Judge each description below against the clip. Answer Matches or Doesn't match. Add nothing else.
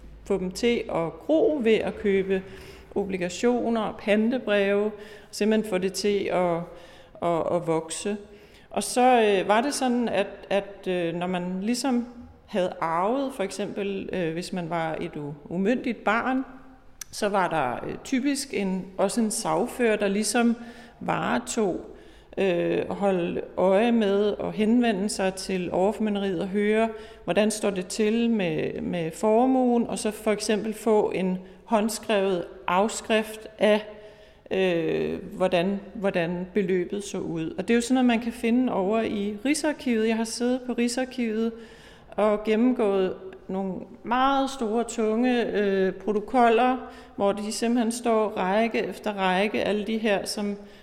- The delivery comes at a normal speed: Doesn't match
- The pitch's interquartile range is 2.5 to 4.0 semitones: Matches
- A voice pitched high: Matches